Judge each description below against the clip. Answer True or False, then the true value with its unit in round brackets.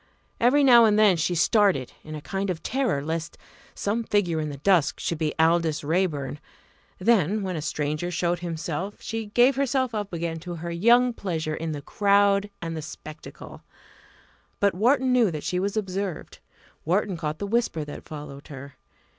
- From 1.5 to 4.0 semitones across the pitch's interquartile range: False (5.0 semitones)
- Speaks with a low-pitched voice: False (180 Hz)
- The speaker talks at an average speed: True (175 wpm)